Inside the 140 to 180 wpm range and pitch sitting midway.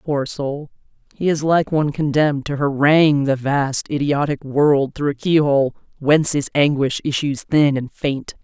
Yes: average, 165 wpm; medium, 145 Hz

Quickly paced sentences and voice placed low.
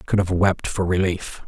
Yes: fast, 245 wpm; very low, 90 Hz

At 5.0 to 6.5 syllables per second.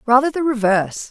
Yes: 6.1 syllables/s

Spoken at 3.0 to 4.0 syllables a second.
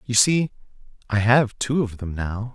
No: 4.2 syllables/s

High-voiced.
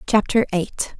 Yes: high, 200 Hz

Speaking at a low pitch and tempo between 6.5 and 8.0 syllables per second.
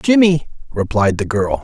No: low, 130 Hz; 4.5 syllables/s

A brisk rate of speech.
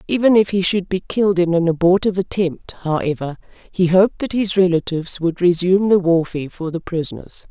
No: average, 185 wpm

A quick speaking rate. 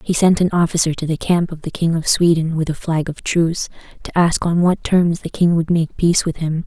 Yes: fast, 260 wpm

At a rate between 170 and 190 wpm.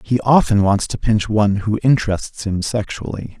Yes: average, 175 wpm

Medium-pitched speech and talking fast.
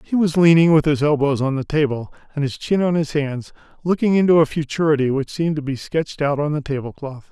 Yes: medium, 150 Hz; fast, 230 wpm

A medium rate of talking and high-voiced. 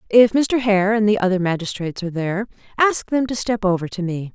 No: fast, 220 wpm; high, 205 Hz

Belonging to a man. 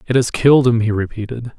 Yes: male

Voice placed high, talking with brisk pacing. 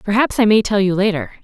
Yes: high, 205 Hz; fast, 250 wpm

